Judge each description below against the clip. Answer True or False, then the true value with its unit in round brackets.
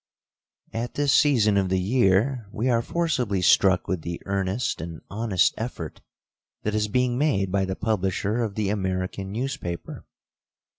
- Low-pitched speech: True (100 Hz)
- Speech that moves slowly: False (150 wpm)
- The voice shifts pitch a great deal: False (4.2 semitones)